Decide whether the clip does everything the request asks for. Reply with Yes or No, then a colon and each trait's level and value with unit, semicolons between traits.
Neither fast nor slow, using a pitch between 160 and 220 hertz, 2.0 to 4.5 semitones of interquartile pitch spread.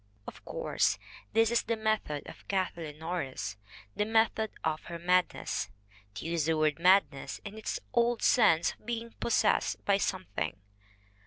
No: average, 150 wpm; medium, 185 Hz; average, 5.3 semitones